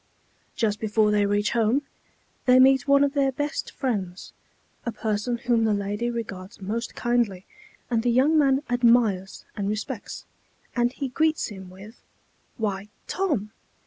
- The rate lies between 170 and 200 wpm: No, average, 145 wpm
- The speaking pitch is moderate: No, high, 230 Hz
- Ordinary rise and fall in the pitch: Yes, average, 3.8 semitones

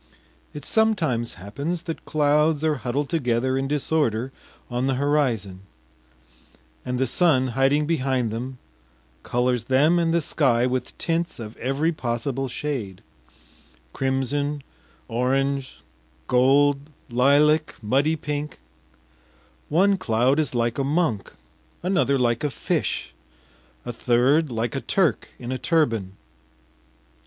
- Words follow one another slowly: Yes, slow, 120 wpm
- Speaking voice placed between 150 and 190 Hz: No, low, 135 Hz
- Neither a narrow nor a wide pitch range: Yes, average, 3.7 semitones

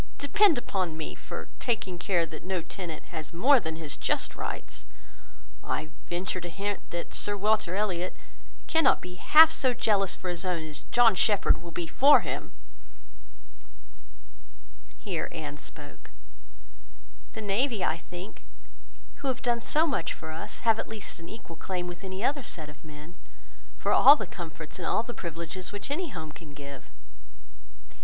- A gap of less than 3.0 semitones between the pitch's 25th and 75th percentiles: No, average, 5.3 semitones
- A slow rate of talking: No, average, 165 wpm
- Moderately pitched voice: Yes, medium, 180 Hz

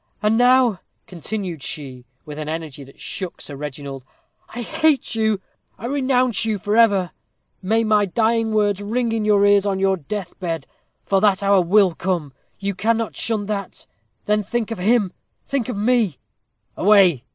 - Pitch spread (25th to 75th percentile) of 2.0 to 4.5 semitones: Yes, average, 3.8 semitones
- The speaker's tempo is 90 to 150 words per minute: No, average, 165 wpm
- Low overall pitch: No, high, 205 Hz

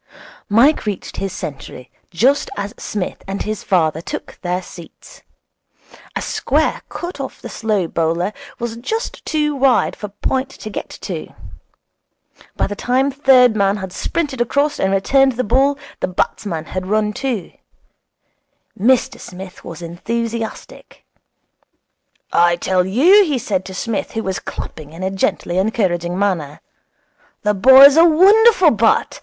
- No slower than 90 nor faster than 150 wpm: Yes, average, 145 wpm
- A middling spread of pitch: No, wide, 6.2 semitones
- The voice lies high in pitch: Yes, high, 215 Hz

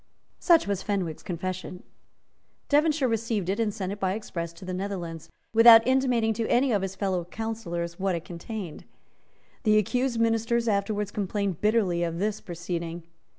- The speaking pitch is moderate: No, high, 200 Hz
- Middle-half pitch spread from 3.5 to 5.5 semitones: Yes, average, 4.1 semitones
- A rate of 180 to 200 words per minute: No, average, 155 wpm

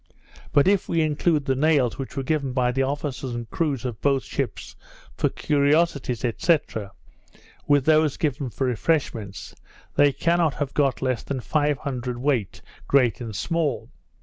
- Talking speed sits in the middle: Yes, average, 155 wpm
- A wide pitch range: No, average, 3.2 semitones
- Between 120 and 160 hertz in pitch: Yes, medium, 140 Hz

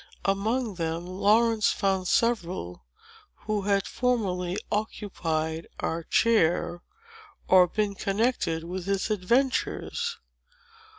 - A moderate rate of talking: No, slow, 95 wpm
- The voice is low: No, high, 195 Hz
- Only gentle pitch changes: No, average, 4.0 semitones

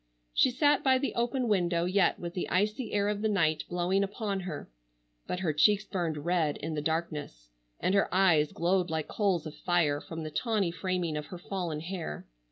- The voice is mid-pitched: Yes, medium, 180 Hz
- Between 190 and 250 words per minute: Yes, average, 195 wpm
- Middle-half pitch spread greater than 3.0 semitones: Yes, average, 4.1 semitones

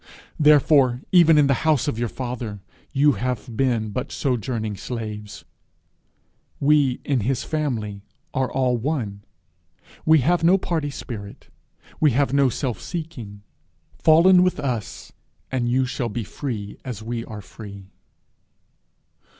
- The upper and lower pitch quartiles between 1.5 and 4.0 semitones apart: No, average, 4.8 semitones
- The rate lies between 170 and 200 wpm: No, slow, 135 wpm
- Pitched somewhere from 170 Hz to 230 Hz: No, low, 125 Hz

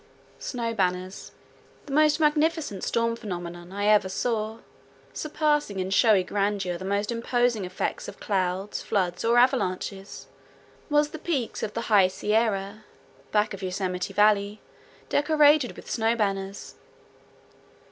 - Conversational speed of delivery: No, slow, 125 wpm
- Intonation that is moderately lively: Yes, average, 4.0 semitones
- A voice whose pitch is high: Yes, high, 210 Hz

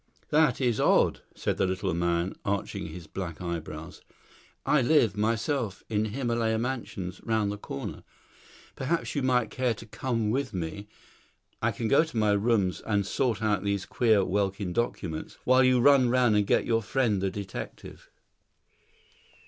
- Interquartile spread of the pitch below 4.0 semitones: No, average, 4.3 semitones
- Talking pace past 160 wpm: No, average, 155 wpm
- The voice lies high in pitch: No, low, 110 Hz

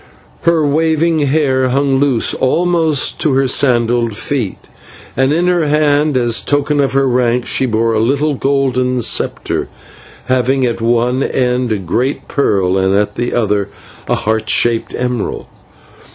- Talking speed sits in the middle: Yes, average, 150 wpm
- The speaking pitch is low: Yes, low, 130 Hz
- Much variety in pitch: No, average, 3.5 semitones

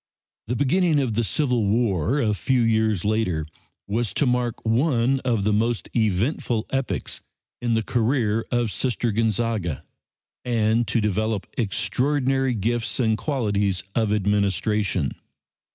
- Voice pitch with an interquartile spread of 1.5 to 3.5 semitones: Yes, average, 2.9 semitones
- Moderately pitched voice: No, low, 115 Hz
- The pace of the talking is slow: Yes, slow, 130 wpm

